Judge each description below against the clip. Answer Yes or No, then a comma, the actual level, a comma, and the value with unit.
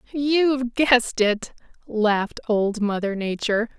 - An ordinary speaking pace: No, slow, 110 wpm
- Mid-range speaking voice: No, high, 230 Hz